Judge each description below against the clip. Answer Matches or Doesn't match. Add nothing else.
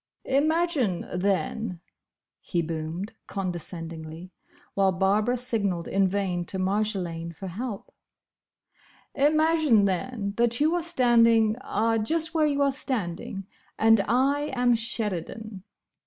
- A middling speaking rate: Doesn't match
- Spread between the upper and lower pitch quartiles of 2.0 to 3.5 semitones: Doesn't match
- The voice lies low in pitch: Doesn't match